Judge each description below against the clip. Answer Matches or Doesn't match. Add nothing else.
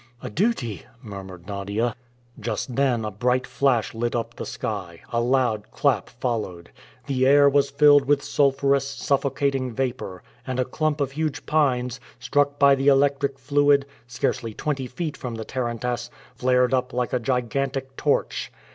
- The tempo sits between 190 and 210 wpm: Doesn't match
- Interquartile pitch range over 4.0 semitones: Doesn't match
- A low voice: Matches